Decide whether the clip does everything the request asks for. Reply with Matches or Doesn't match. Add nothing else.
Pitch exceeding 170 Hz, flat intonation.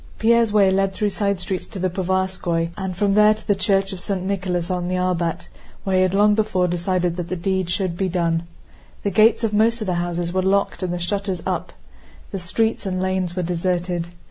Matches